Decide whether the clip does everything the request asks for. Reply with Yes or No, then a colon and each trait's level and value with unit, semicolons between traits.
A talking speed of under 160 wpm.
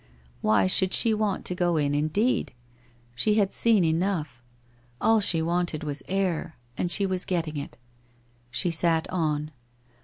Yes: average, 150 wpm